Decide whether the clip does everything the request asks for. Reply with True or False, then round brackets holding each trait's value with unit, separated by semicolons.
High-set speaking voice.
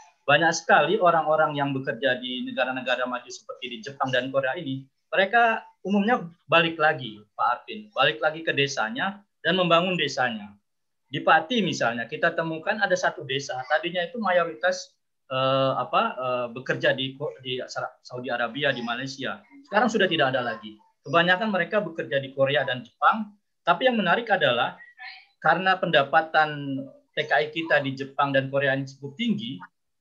False (155 Hz)